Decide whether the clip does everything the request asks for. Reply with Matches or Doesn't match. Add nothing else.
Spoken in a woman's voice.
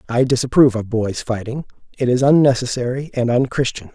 Doesn't match